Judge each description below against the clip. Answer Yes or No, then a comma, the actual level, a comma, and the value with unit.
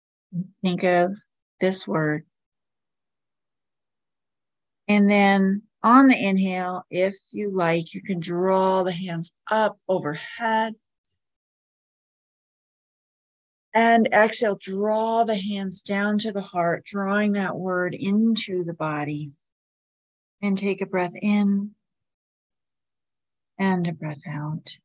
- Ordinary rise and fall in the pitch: Yes, average, 3.3 semitones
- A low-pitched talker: No, high, 190 Hz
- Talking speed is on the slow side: Yes, slow, 105 wpm